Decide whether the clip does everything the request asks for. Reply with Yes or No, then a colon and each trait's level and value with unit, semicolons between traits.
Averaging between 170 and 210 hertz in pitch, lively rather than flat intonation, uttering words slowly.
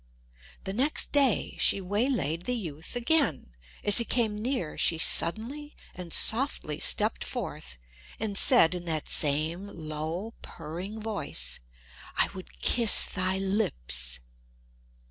Yes: high, 190 Hz; wide, 6.5 semitones; slow, 125 wpm